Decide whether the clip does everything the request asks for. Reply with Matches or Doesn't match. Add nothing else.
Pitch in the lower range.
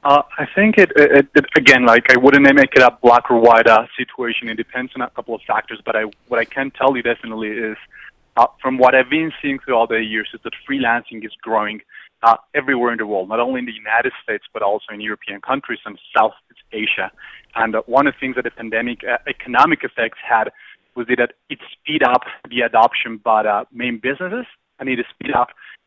Matches